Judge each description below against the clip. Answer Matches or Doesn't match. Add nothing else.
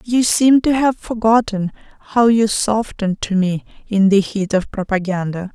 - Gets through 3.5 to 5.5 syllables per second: Matches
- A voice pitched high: Matches